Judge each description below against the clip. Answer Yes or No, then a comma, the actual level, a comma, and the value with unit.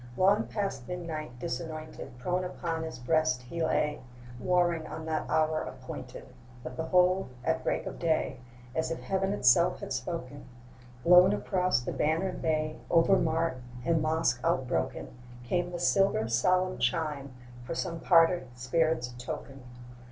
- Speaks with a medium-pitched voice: Yes, medium, 160 Hz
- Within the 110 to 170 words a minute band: Yes, average, 140 wpm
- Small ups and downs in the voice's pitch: No, average, 4.1 semitones